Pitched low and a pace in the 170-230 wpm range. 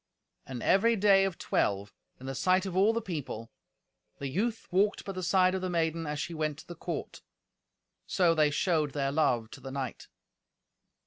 No: medium, 165 Hz; average, 190 wpm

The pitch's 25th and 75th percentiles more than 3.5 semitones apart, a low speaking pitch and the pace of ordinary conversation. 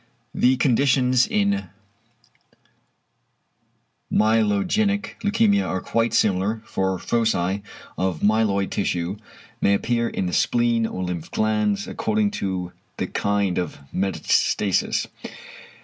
No: average, 5.2 semitones; low, 110 Hz; slow, 100 wpm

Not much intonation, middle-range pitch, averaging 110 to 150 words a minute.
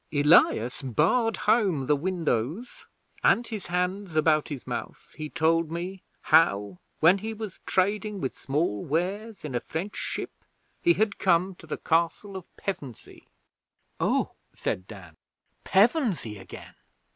No: wide, 5.4 semitones; medium, 170 Hz; slow, 135 wpm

